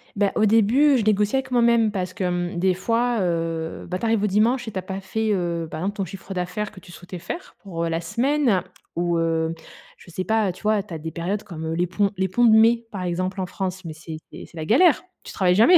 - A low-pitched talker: No, high, 190 Hz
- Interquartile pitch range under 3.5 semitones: No, average, 4.1 semitones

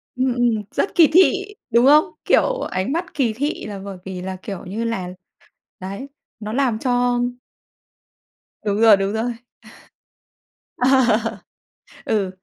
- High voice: Yes, high, 230 Hz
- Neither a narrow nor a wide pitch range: Yes, average, 4.7 semitones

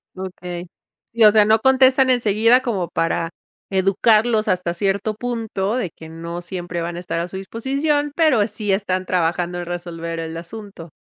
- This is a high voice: Yes, high, 195 Hz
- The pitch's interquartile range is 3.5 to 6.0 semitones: Yes, average, 4.6 semitones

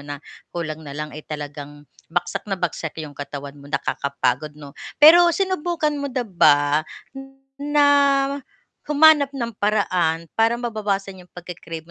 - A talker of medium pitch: Yes, medium, 175 Hz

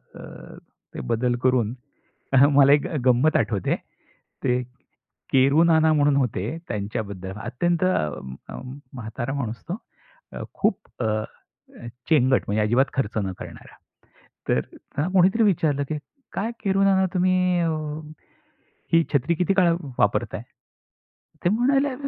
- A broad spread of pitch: Yes, wide, 6.1 semitones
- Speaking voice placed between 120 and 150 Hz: Yes, medium, 140 Hz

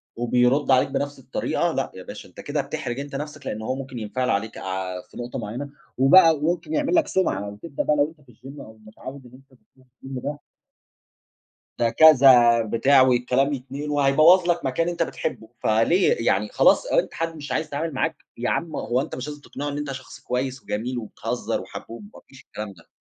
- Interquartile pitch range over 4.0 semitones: No, average, 3.6 semitones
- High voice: No, low, 135 Hz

